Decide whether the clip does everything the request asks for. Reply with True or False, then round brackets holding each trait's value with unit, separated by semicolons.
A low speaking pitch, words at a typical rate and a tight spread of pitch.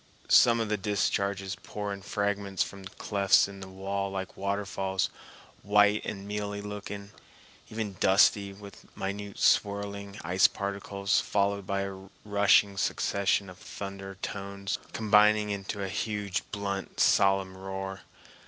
False (100 Hz; 130 wpm; 0.9 semitones)